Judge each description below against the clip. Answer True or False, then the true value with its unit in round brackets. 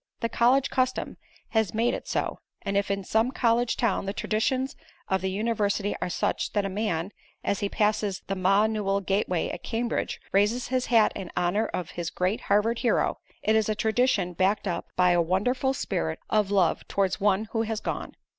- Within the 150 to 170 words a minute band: False (195 wpm)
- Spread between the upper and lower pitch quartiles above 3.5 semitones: False (3.0 semitones)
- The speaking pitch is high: True (210 Hz)